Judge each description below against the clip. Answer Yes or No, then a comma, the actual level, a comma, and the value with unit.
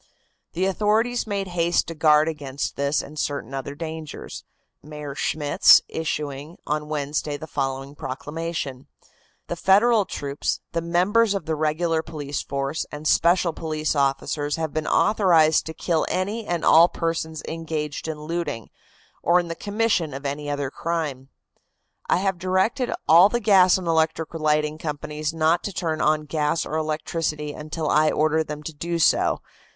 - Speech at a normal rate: Yes, average, 155 wpm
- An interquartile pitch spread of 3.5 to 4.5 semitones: No, narrow, 2.5 semitones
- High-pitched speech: No, medium, 160 Hz